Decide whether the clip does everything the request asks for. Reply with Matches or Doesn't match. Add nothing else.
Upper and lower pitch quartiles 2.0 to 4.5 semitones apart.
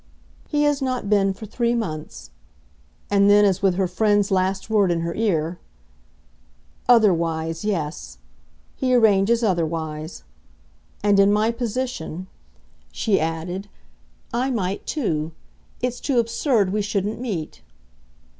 Doesn't match